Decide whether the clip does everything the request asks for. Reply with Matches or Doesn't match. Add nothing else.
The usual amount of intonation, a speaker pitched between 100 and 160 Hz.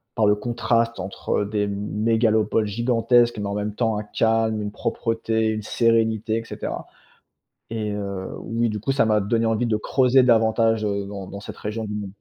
Doesn't match